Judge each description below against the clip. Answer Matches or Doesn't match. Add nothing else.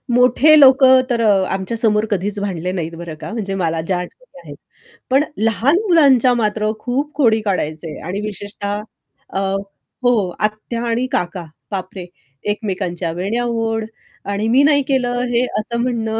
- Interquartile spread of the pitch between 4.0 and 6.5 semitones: Matches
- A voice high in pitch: Matches